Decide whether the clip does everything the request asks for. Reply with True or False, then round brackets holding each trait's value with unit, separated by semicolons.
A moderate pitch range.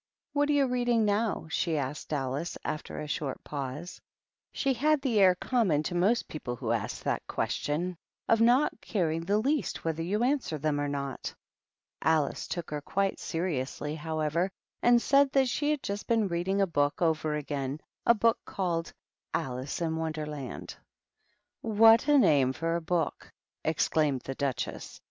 False (7.2 semitones)